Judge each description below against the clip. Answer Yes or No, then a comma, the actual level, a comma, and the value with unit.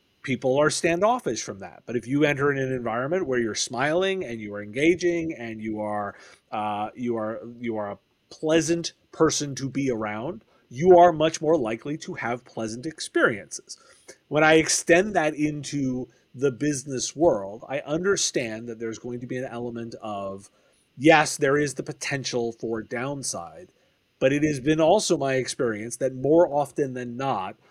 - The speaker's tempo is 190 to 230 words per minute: No, average, 170 wpm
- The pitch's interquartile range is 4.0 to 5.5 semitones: Yes, average, 5.0 semitones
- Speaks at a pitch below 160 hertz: Yes, low, 135 Hz